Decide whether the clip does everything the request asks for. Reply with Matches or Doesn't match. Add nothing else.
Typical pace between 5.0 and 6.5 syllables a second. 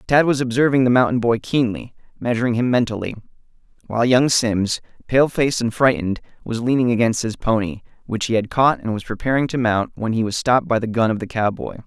Matches